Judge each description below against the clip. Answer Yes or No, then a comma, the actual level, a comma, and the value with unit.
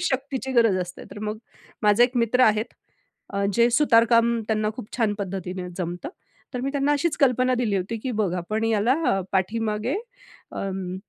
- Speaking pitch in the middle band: No, high, 225 Hz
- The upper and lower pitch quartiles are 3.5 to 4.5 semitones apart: Yes, average, 3.8 semitones